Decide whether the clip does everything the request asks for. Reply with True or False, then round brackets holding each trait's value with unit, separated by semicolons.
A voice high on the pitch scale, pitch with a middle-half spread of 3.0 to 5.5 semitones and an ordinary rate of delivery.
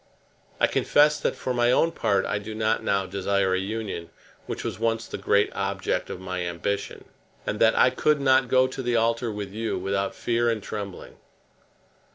False (110 Hz; 3.5 semitones; 190 wpm)